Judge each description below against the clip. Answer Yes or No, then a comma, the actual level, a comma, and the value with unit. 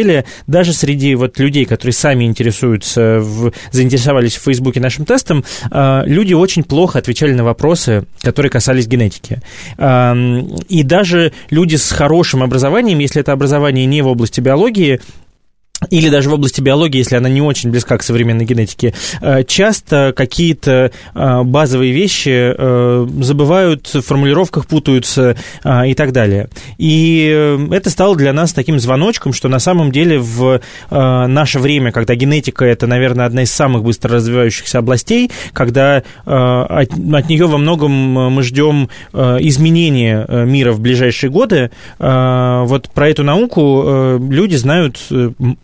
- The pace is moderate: Yes, average, 135 wpm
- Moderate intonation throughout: Yes, average, 3.3 semitones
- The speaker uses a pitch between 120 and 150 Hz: Yes, low, 135 Hz